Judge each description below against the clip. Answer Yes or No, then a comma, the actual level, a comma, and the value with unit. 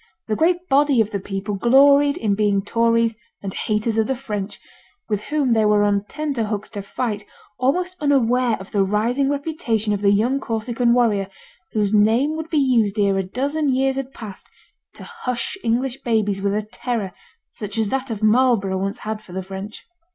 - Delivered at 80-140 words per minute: No, average, 190 wpm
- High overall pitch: Yes, high, 225 Hz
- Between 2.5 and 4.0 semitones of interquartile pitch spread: No, average, 4.4 semitones